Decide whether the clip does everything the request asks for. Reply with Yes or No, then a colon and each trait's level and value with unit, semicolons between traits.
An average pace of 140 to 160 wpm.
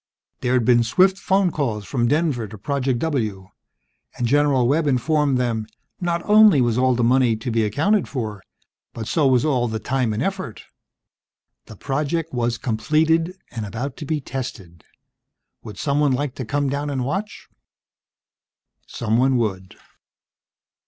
Yes: average, 150 wpm